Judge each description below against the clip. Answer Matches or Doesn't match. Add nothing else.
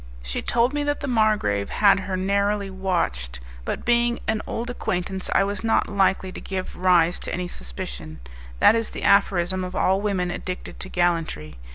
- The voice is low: Doesn't match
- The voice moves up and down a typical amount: Matches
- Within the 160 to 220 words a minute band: Matches